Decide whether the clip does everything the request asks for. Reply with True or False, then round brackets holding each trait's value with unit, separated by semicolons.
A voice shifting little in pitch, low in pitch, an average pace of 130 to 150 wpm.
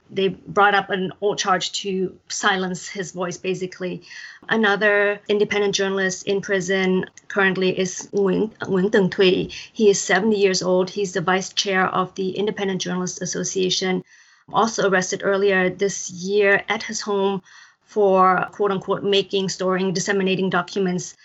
False (1.3 semitones; 195 Hz; 140 wpm)